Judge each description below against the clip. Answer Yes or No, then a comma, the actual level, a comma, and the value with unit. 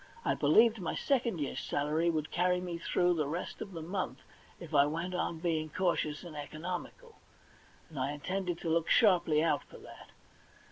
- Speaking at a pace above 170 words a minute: Yes, average, 180 wpm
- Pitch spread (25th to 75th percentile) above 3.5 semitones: No, average, 2.9 semitones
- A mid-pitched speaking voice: Yes, medium, 170 Hz